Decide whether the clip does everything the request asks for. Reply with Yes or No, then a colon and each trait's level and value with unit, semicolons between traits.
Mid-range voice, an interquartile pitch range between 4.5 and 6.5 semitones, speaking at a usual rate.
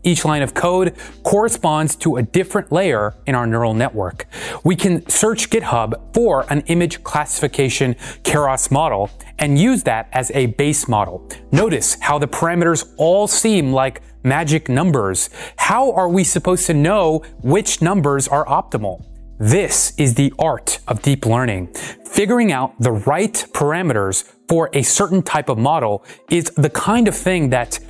Yes: medium, 155 Hz; wide, 5.6 semitones; average, 155 wpm